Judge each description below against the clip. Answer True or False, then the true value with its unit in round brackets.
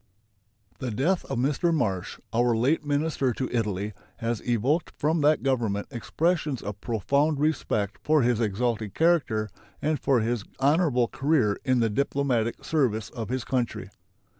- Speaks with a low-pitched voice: True (125 Hz)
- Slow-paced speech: False (145 wpm)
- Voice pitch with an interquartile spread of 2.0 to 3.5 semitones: False (4.8 semitones)